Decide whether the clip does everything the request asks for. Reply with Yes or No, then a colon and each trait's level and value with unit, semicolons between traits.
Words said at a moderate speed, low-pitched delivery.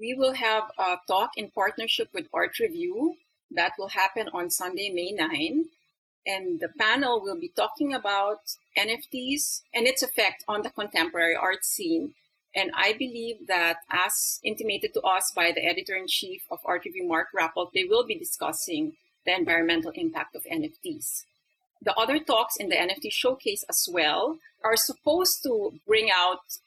No: average, 165 wpm; high, 245 Hz